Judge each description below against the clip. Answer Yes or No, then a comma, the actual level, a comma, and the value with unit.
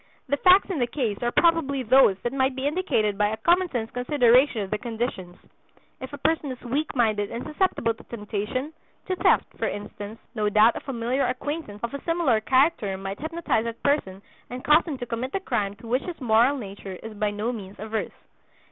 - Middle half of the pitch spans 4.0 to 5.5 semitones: Yes, average, 5.0 semitones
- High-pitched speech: Yes, high, 245 Hz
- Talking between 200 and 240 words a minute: Yes, fast, 205 wpm